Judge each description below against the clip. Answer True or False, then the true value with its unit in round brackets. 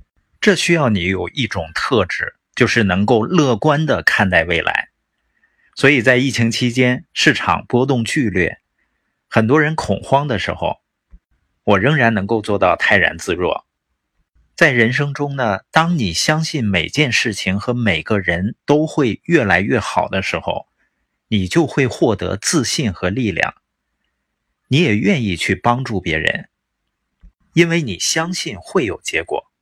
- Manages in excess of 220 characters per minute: False (215 characters per minute)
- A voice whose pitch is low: True (120 Hz)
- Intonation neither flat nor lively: False (6.8 semitones)